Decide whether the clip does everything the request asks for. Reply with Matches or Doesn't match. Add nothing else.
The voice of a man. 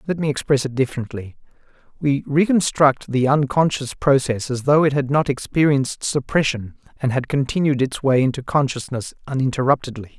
Matches